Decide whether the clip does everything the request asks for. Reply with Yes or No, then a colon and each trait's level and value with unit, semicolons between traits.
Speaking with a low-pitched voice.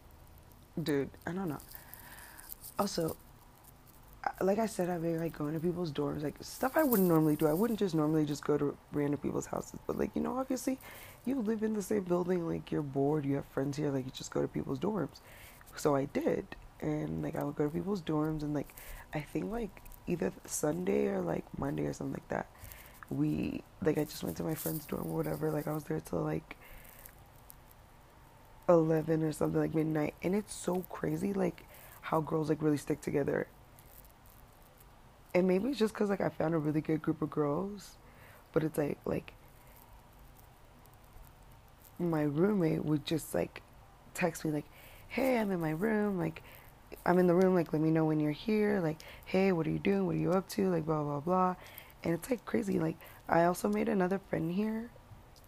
No: medium, 160 Hz